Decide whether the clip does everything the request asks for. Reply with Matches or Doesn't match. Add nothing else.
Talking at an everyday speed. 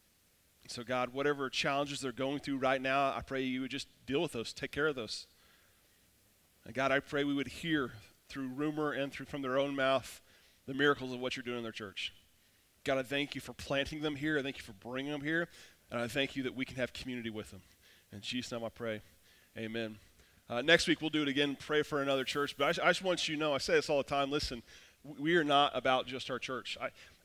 Doesn't match